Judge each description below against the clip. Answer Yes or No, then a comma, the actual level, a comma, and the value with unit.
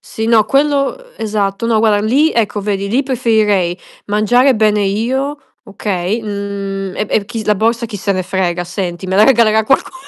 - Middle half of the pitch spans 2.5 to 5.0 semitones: Yes, average, 2.9 semitones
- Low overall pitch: No, high, 215 Hz